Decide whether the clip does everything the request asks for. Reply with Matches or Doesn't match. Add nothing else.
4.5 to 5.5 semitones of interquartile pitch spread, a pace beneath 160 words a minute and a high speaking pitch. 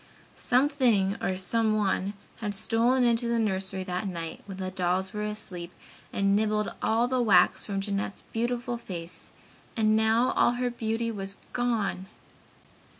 Doesn't match